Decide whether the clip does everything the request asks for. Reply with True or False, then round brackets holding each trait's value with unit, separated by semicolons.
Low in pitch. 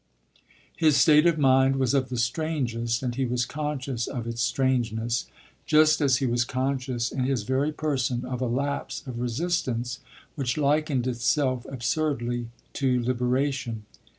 True (130 Hz)